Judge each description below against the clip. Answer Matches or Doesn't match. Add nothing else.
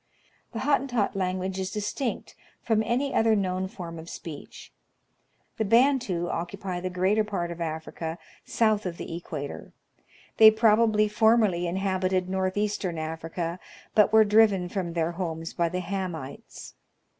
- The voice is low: Doesn't match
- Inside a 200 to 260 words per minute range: Doesn't match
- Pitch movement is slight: Doesn't match